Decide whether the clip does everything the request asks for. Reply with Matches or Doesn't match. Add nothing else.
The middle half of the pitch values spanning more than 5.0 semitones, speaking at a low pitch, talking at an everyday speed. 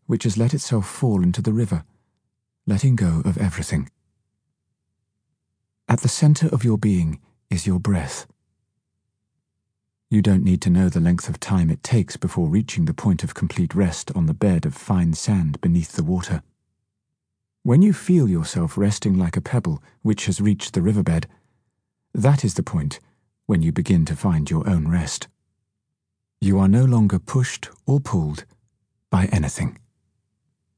Matches